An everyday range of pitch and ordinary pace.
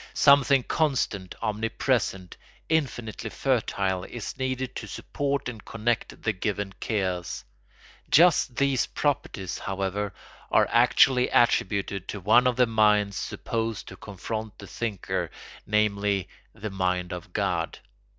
No: average, 4.2 semitones; slow, 120 wpm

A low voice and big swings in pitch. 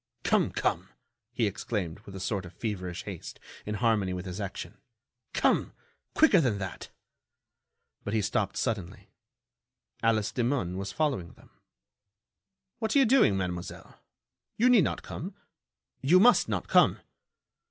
Yes: low, 105 Hz; wide, 7.0 semitones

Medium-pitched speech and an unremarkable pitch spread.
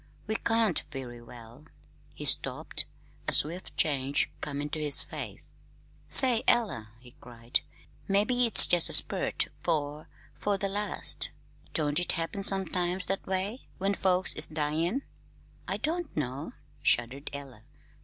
No: medium, 165 Hz; wide, 5.9 semitones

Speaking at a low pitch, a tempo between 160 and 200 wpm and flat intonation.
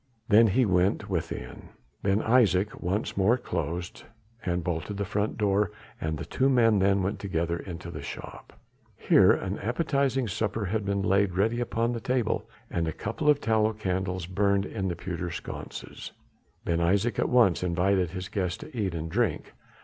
No: low, 100 Hz; average, 170 wpm; average, 3.8 semitones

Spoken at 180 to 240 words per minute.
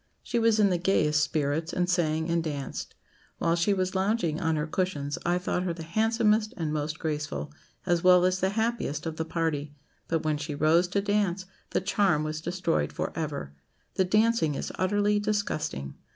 Yes: average, 185 wpm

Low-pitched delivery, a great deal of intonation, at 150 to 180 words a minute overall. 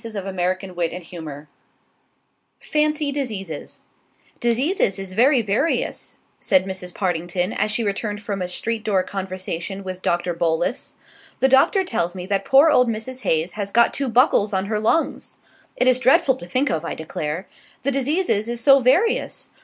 No: high, 210 Hz; wide, 5.8 semitones; average, 160 wpm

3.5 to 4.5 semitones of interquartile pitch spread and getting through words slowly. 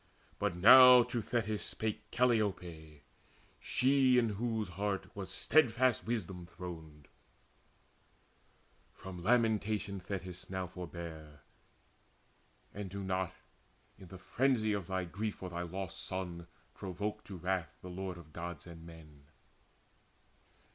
Yes: average, 3.9 semitones; slow, 120 wpm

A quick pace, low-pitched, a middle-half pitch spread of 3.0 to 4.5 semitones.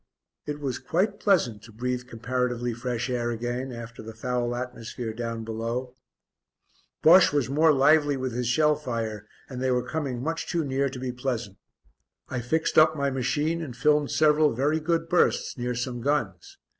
No: average, 170 wpm; low, 125 Hz; average, 3.8 semitones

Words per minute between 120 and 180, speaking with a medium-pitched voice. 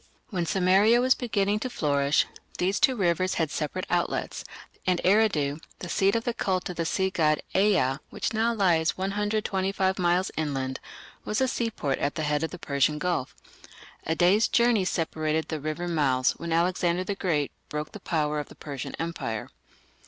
Yes: average, 175 wpm; medium, 175 Hz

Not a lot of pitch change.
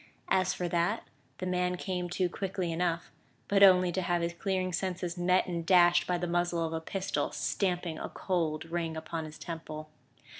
Yes: narrow, 1.6 semitones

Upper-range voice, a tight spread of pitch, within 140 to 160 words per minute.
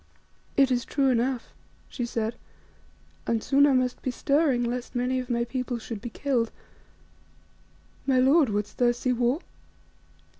Yes: very high, 250 Hz; narrow, 2.0 semitones; average, 150 wpm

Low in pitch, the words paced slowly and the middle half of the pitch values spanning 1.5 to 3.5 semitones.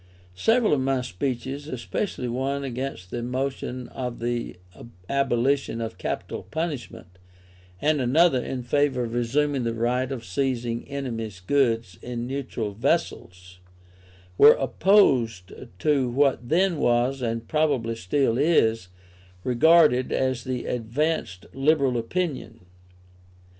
Yes: low, 125 Hz; slow, 115 wpm; average, 3.2 semitones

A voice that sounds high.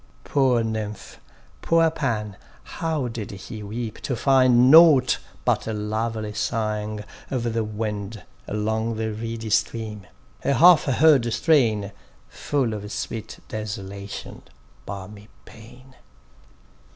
No: low, 110 Hz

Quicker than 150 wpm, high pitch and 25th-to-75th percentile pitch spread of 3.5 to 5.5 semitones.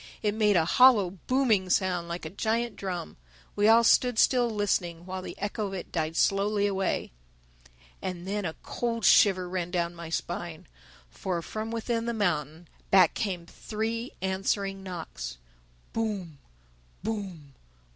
No: average, 145 wpm; high, 195 Hz; average, 3.9 semitones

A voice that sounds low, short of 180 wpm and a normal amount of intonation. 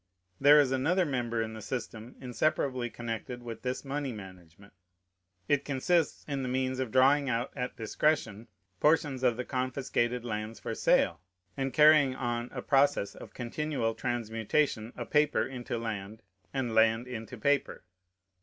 Yes: low, 125 Hz; average, 150 wpm; average, 3.3 semitones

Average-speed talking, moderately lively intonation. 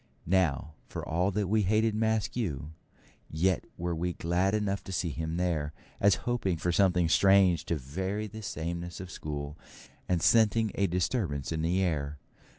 Yes: average, 160 wpm; average, 3.7 semitones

